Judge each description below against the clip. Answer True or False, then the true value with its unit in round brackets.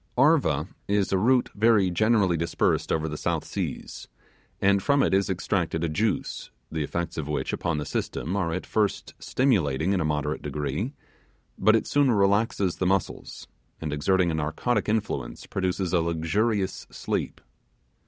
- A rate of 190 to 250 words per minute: False (160 wpm)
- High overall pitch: False (95 Hz)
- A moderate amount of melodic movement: True (4.8 semitones)